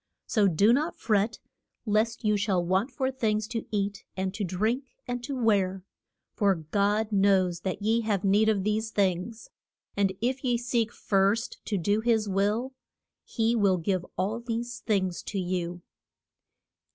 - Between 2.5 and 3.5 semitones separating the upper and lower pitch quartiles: Yes, average, 3.0 semitones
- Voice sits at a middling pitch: No, high, 210 Hz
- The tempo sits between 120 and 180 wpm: Yes, average, 160 wpm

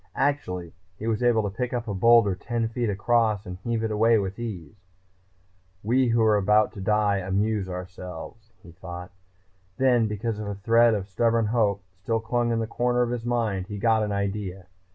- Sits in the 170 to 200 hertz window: No, low, 110 Hz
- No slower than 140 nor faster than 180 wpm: No, average, 190 wpm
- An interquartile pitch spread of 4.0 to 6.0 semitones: No, average, 3.0 semitones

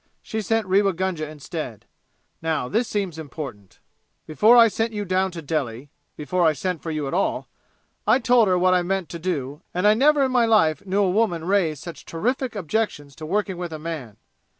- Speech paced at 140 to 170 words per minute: No, average, 200 wpm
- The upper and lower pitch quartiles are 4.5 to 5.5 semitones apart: Yes, average, 5.2 semitones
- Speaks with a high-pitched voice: No, medium, 180 Hz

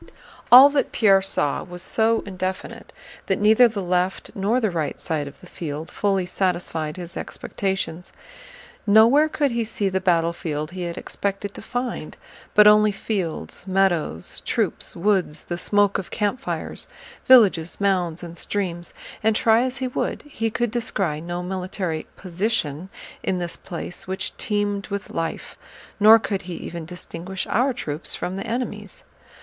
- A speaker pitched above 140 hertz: Yes, high, 190 Hz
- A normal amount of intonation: Yes, average, 3.7 semitones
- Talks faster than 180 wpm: No, average, 155 wpm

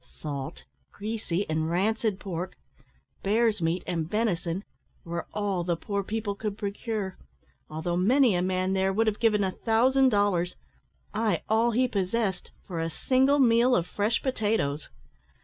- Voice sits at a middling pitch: No, high, 200 Hz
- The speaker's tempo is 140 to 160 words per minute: Yes, average, 150 wpm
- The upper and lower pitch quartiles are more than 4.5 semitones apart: No, average, 4.0 semitones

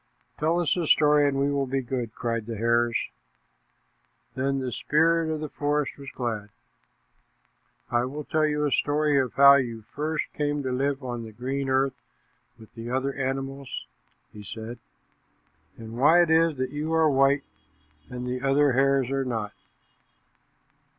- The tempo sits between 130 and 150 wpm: No, average, 165 wpm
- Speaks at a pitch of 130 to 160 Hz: Yes, low, 135 Hz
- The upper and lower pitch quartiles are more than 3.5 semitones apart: No, average, 3.1 semitones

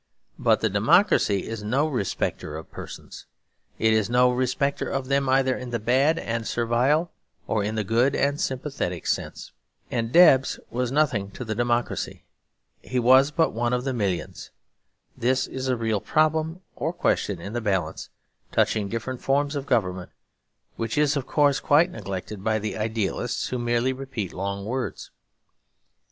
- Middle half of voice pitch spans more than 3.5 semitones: Yes, average, 3.9 semitones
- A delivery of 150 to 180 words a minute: Yes, average, 155 wpm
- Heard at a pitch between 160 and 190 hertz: No, low, 120 Hz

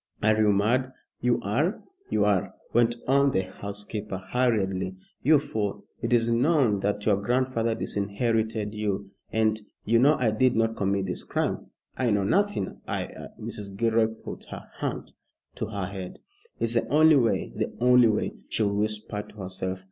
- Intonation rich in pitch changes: No, average, 3.1 semitones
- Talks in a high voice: No, low, 110 Hz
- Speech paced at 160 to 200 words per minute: Yes, average, 170 wpm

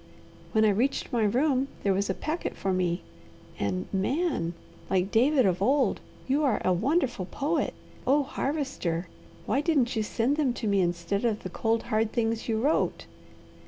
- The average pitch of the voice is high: Yes, high, 225 Hz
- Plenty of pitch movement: Yes, wide, 6.2 semitones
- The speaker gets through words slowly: No, average, 170 wpm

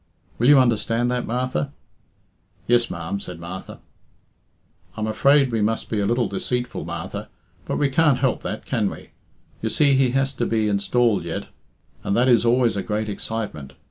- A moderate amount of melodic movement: Yes, average, 3.8 semitones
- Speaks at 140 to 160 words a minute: No, average, 175 wpm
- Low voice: Yes, low, 115 Hz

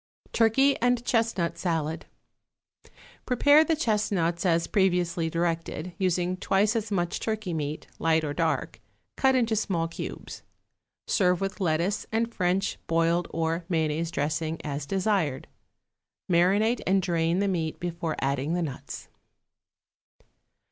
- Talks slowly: Yes, slow, 125 wpm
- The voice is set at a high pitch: No, medium, 175 Hz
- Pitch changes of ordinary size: Yes, average, 4.0 semitones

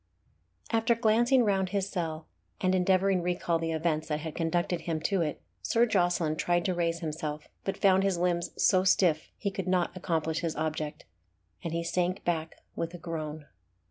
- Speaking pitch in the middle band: Yes, medium, 175 Hz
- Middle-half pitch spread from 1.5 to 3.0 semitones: Yes, average, 2.7 semitones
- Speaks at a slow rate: No, average, 180 wpm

